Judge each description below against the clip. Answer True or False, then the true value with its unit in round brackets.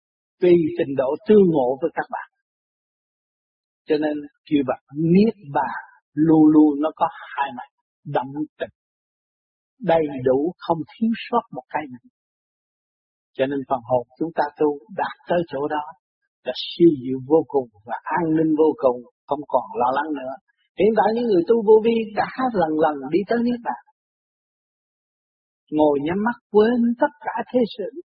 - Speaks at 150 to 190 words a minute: True (170 wpm)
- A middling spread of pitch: False (7.6 semitones)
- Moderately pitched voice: True (160 Hz)